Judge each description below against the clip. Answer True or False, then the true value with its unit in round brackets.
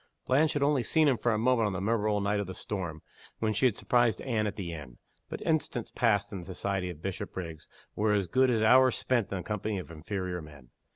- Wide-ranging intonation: False (4.8 semitones)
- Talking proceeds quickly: True (235 wpm)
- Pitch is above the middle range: False (105 Hz)